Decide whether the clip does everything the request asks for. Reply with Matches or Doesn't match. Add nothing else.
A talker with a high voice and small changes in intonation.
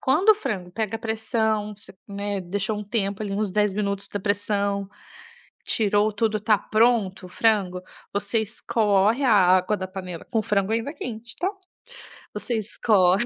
Matches